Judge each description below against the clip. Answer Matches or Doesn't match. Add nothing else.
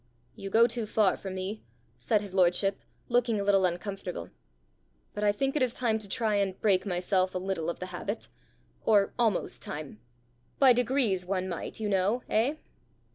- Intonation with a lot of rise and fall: Doesn't match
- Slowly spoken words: Doesn't match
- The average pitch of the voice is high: Matches